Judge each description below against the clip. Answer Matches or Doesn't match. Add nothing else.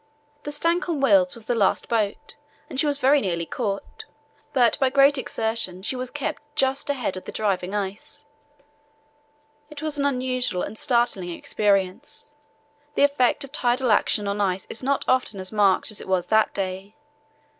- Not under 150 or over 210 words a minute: Matches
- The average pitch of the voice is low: Doesn't match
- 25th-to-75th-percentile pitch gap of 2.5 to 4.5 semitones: Doesn't match